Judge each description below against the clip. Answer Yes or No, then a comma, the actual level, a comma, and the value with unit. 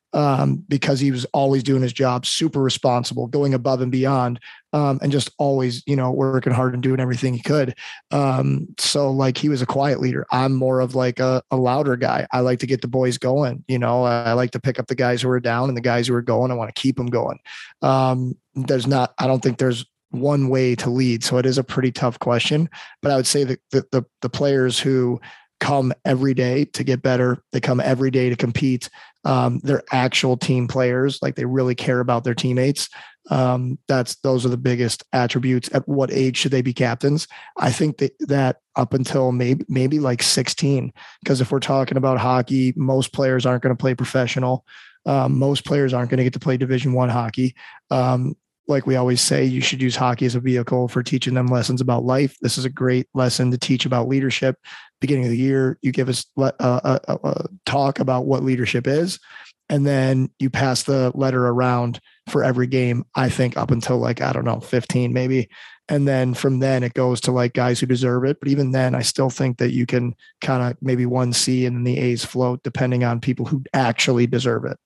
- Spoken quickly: Yes, fast, 220 wpm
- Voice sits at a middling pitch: No, low, 130 Hz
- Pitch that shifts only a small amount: Yes, narrow, 1.3 semitones